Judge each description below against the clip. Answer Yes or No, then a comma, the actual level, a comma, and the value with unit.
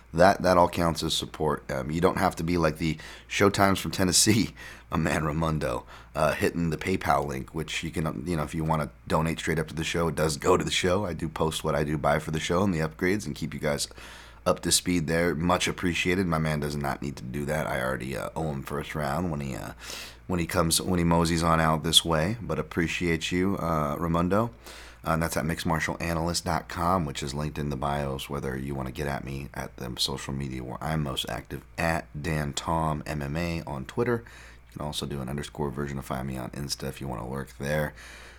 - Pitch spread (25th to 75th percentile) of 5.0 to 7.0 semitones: No, average, 2.9 semitones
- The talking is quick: Yes, fast, 240 wpm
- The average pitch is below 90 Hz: Yes, very low, 80 Hz